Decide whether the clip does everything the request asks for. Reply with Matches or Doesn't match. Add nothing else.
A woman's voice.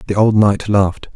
Doesn't match